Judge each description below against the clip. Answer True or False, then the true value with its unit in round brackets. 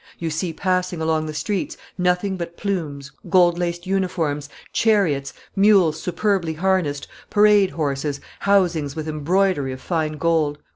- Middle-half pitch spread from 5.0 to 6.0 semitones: False (3.8 semitones)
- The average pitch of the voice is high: False (170 Hz)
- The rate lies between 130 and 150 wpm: True (135 wpm)